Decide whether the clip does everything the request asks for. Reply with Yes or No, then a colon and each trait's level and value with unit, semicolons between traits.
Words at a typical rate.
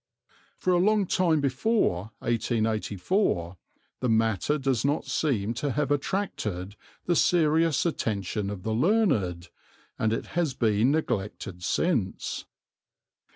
No: slow, 115 wpm